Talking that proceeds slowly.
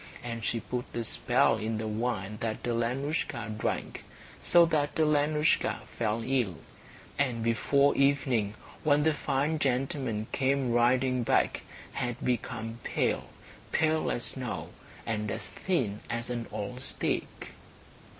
Yes: slow, 130 wpm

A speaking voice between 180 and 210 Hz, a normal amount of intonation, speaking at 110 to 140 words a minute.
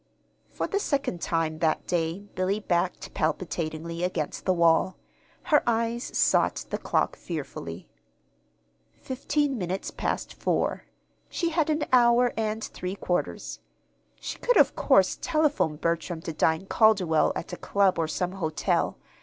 No: medium, 185 Hz; wide, 6.2 semitones; slow, 135 wpm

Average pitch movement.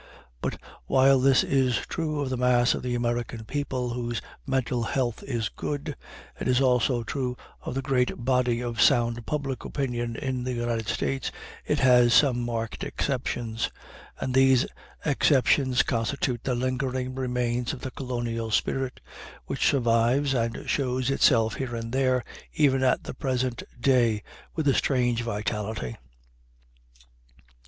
No: narrow, 1.9 semitones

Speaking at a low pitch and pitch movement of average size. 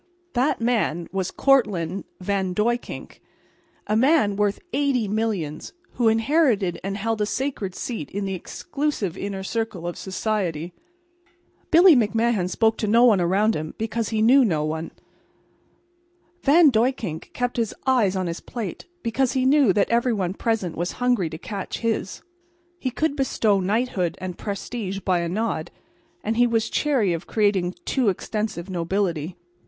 No: high, 210 Hz; average, 4.4 semitones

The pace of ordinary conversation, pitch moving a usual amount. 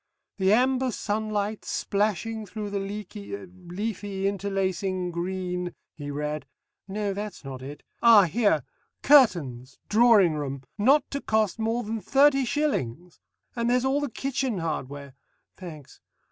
No: slow, 130 wpm; average, 4.4 semitones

